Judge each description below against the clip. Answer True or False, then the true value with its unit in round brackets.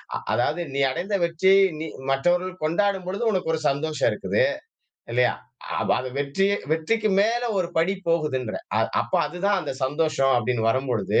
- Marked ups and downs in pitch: True (5.7 semitones)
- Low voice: False (160 Hz)